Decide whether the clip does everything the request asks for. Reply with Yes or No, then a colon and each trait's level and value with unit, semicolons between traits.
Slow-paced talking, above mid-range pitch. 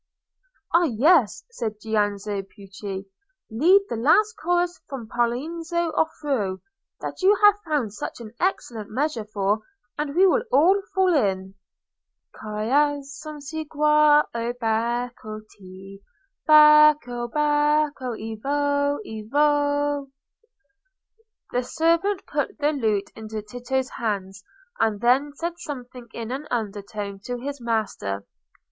Yes: slow, 115 wpm; very high, 255 Hz